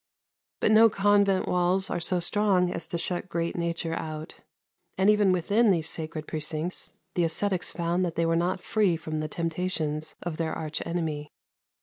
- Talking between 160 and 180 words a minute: Yes, average, 175 wpm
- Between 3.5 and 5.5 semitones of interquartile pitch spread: No, narrow, 2.6 semitones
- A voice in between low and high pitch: Yes, medium, 170 Hz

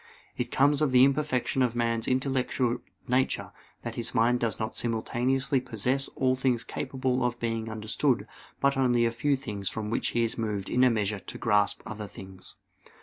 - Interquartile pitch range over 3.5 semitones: No, average, 2.8 semitones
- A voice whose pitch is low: Yes, low, 120 Hz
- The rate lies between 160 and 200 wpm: Yes, average, 180 wpm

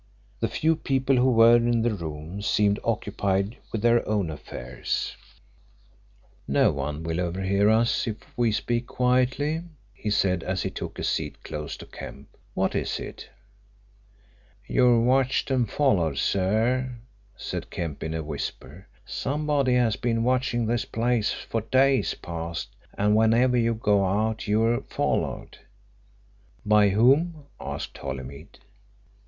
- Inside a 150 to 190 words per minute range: No, slow, 135 wpm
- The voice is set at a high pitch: No, low, 110 Hz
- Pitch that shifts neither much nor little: Yes, average, 4.5 semitones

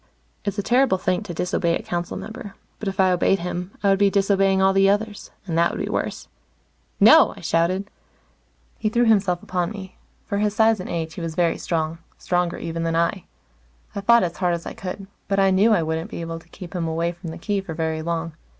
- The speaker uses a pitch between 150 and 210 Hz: Yes, medium, 185 Hz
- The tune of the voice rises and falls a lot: No, average, 2.9 semitones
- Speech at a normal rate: No, fast, 230 wpm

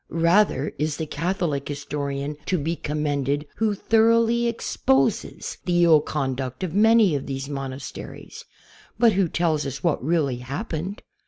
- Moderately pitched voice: Yes, medium, 155 Hz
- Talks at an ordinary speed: Yes, average, 145 wpm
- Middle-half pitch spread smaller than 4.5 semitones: No, average, 4.8 semitones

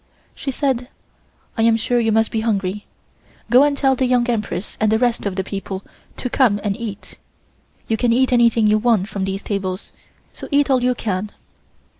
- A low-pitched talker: No, high, 225 Hz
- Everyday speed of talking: Yes, average, 195 wpm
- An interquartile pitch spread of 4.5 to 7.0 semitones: No, average, 3.4 semitones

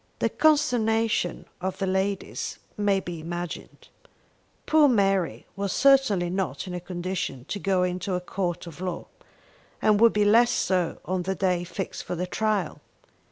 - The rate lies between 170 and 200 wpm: No, average, 160 wpm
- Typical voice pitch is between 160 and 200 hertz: Yes, high, 190 Hz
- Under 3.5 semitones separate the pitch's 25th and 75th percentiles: Yes, average, 2.8 semitones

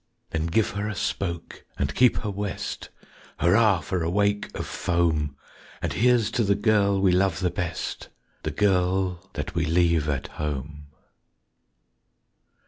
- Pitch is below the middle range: Yes, very low, 90 Hz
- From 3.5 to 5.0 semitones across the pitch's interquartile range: Yes, average, 3.8 semitones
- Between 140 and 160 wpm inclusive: Yes, average, 145 wpm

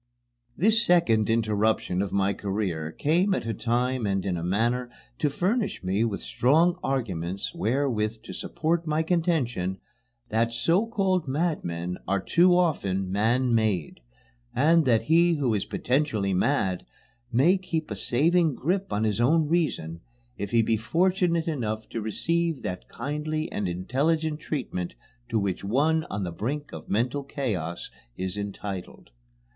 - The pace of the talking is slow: No, average, 150 wpm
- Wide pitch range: Yes, wide, 8.0 semitones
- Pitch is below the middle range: Yes, low, 120 Hz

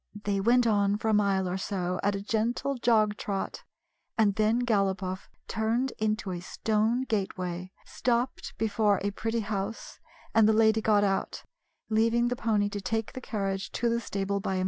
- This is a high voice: Yes, high, 215 Hz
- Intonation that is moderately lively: No, narrow, 2.3 semitones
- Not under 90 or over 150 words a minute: No, average, 175 wpm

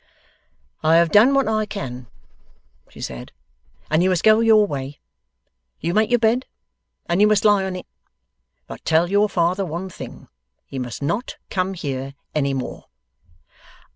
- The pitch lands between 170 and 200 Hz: Yes, medium, 185 Hz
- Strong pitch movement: Yes, wide, 6.3 semitones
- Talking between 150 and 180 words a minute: Yes, average, 160 wpm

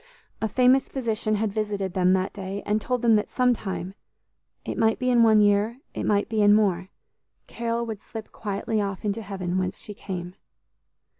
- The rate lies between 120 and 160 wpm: No, average, 180 wpm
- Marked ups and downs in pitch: No, narrow, 2.6 semitones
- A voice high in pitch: Yes, high, 210 Hz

